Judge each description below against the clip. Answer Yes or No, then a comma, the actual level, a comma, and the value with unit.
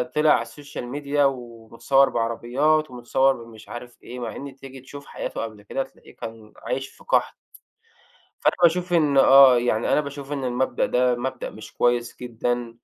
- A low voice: Yes, low, 130 Hz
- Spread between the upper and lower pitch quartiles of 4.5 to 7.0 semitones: No, average, 2.8 semitones